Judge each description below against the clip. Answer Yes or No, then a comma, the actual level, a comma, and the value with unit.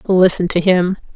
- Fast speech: No, average, 155 wpm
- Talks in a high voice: No, medium, 180 Hz